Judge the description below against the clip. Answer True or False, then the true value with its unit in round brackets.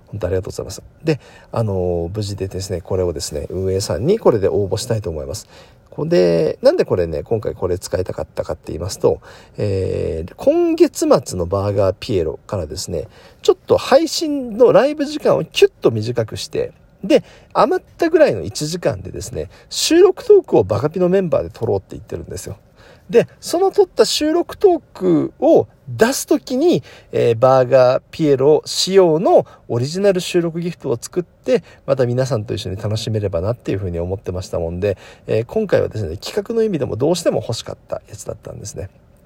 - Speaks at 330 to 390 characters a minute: False (400 characters per minute)